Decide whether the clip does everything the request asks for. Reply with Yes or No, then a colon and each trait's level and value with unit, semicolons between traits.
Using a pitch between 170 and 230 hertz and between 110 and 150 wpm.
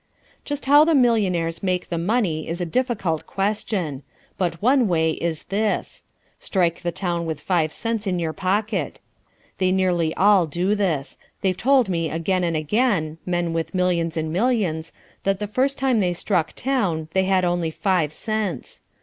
No: medium, 185 Hz; average, 165 wpm